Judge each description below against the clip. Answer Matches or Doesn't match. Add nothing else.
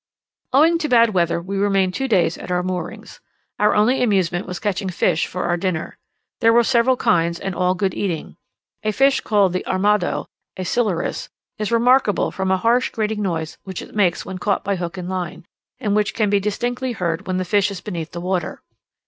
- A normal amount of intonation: Matches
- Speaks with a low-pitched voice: Doesn't match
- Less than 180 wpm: Doesn't match